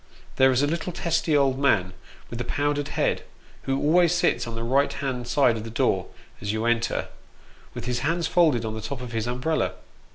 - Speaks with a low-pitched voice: Yes, low, 130 Hz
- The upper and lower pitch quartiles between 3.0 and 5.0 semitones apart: Yes, average, 3.9 semitones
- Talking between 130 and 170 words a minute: No, fast, 205 wpm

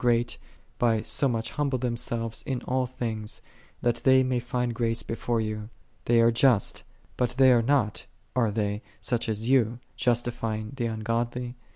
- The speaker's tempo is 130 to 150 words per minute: No, average, 160 wpm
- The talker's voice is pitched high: No, low, 120 Hz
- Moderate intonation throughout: No, narrow, 1.7 semitones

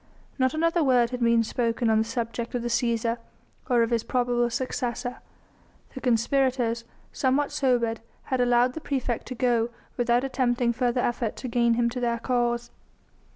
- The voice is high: Yes, high, 240 Hz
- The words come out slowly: No, average, 165 wpm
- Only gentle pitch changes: Yes, narrow, 1.4 semitones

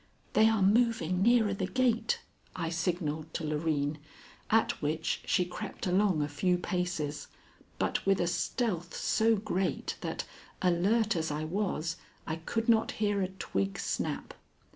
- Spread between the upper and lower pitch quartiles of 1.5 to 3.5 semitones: No, average, 4.9 semitones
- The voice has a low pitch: No, medium, 180 Hz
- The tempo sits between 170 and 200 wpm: No, average, 145 wpm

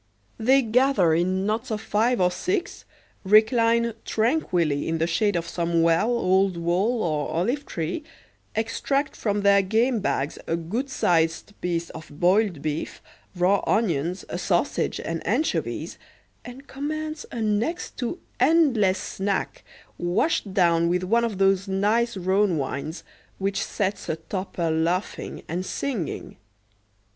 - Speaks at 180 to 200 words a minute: No, slow, 135 wpm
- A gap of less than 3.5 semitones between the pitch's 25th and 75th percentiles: No, average, 5.2 semitones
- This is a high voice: Yes, high, 195 Hz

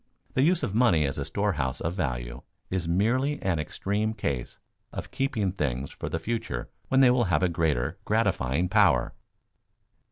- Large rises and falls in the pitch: Yes, wide, 8.4 semitones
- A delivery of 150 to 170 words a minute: Yes, average, 165 wpm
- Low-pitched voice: Yes, very low, 90 Hz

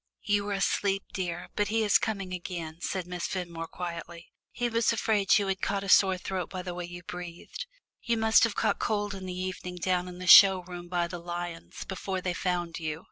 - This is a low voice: No, medium, 185 Hz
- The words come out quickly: Yes, fast, 215 wpm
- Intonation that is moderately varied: No, narrow, 2.2 semitones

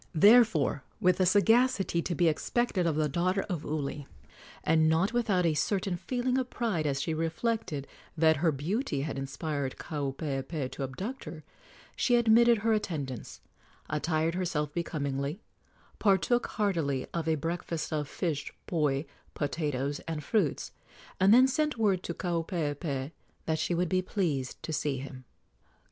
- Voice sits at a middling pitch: Yes, medium, 165 Hz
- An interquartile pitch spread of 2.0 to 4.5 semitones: No, average, 5.1 semitones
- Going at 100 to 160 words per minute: Yes, average, 150 wpm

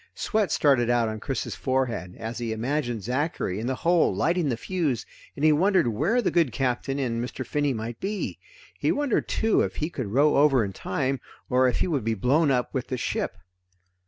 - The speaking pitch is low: Yes, low, 130 Hz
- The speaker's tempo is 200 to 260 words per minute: Yes, fast, 205 wpm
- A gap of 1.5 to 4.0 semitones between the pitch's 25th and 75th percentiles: No, average, 4.6 semitones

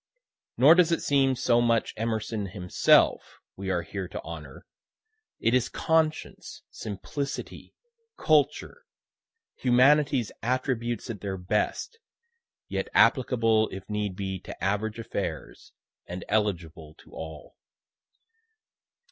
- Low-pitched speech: Yes, low, 110 Hz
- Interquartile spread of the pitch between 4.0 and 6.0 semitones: Yes, average, 5.3 semitones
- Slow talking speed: Yes, slow, 110 wpm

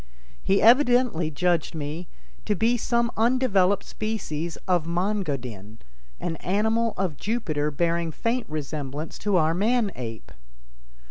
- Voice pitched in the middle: Yes, medium, 180 Hz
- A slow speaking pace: Yes, slow, 130 wpm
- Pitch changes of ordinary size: No, wide, 6.2 semitones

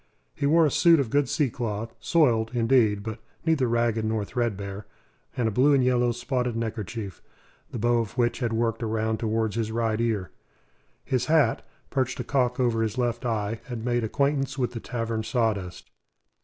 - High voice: No, low, 115 Hz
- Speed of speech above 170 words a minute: Yes, average, 180 wpm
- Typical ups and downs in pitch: No, narrow, 2.2 semitones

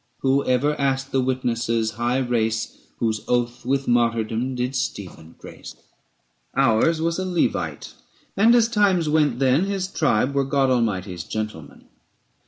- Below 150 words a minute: Yes, average, 140 wpm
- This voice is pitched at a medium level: No, low, 130 Hz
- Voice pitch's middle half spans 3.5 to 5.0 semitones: Yes, average, 4.0 semitones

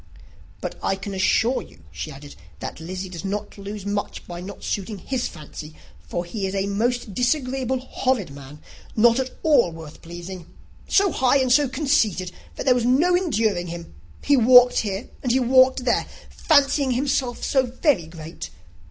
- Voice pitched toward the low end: No, high, 220 Hz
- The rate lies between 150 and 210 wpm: Yes, average, 170 wpm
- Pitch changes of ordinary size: No, wide, 6.3 semitones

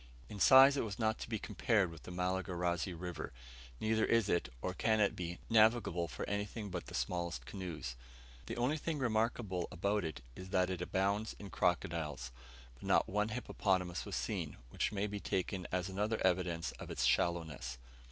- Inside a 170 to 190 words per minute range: Yes, average, 180 wpm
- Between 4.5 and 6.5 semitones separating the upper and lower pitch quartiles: No, average, 3.8 semitones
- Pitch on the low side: Yes, very low, 95 Hz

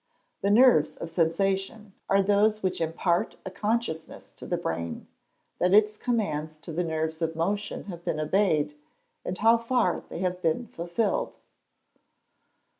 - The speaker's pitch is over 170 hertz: Yes, medium, 185 Hz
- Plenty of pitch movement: No, average, 4.5 semitones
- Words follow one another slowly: No, average, 150 wpm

